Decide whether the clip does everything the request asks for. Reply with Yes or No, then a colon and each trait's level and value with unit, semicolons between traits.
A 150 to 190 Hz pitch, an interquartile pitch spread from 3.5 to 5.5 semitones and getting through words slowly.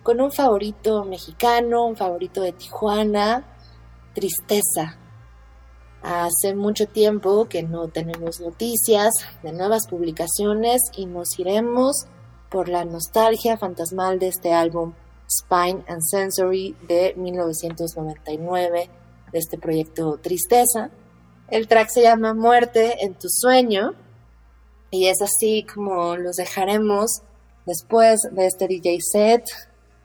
Yes: medium, 185 Hz; average, 4.4 semitones; slow, 115 wpm